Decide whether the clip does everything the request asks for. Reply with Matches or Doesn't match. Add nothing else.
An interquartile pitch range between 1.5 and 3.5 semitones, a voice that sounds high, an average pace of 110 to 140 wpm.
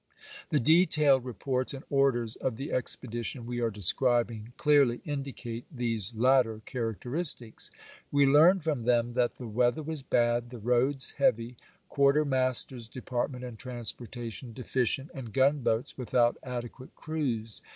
Doesn't match